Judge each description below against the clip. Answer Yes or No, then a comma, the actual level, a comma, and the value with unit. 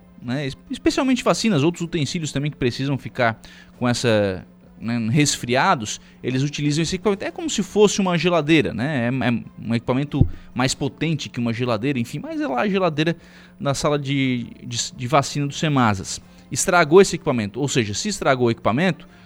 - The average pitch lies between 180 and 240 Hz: No, medium, 140 Hz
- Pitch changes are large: Yes, wide, 6.2 semitones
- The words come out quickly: No, average, 175 wpm